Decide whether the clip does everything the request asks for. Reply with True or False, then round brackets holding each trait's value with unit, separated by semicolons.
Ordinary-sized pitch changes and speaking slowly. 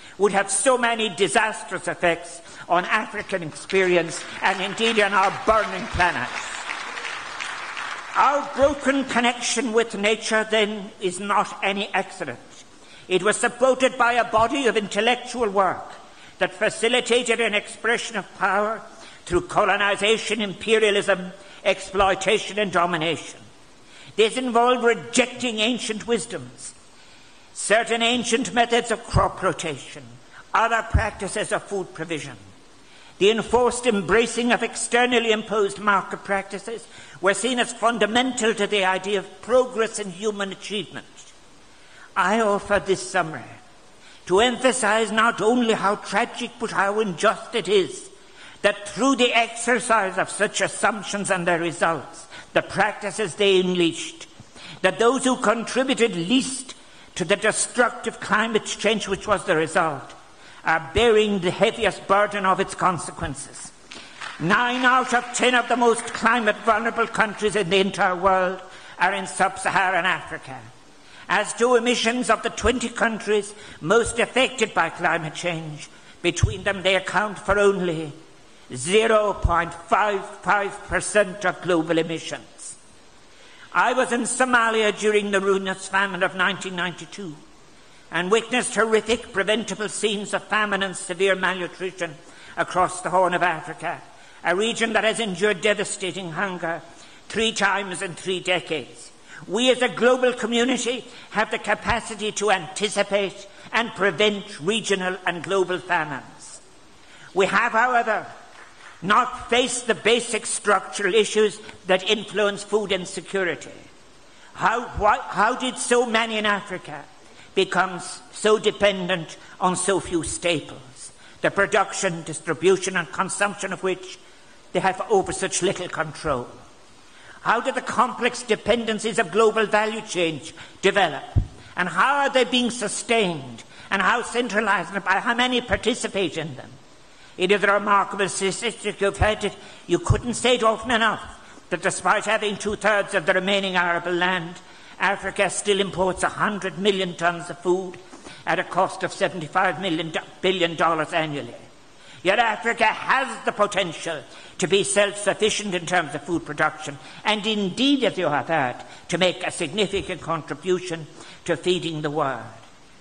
True (3.5 semitones; 130 wpm)